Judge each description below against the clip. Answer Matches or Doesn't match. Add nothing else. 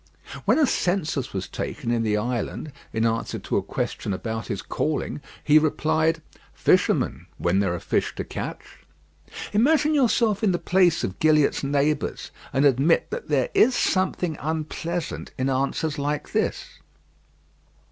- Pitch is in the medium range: Matches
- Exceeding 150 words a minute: Doesn't match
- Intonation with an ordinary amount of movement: Doesn't match